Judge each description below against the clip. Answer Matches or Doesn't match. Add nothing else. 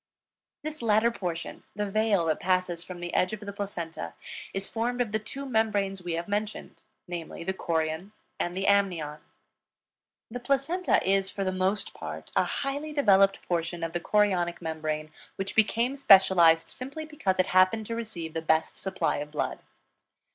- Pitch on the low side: Doesn't match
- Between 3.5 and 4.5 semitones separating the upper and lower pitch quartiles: Matches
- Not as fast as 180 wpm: Matches